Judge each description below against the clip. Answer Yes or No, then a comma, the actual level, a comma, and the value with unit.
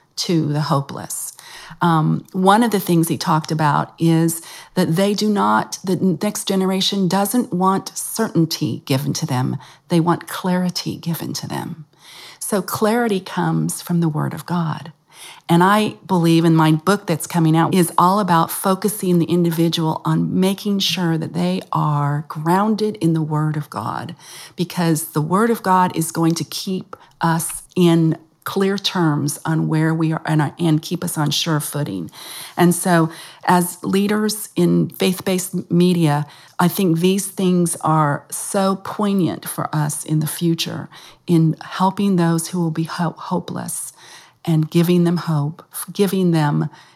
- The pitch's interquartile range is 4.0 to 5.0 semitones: No, average, 2.9 semitones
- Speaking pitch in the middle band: Yes, medium, 170 Hz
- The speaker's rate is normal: Yes, average, 155 wpm